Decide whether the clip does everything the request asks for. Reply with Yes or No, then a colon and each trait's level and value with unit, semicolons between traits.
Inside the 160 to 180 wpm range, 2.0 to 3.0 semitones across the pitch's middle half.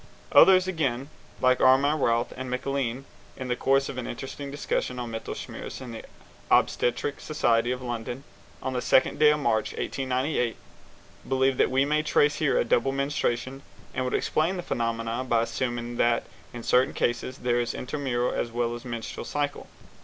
Yes: average, 175 wpm; narrow, 2.5 semitones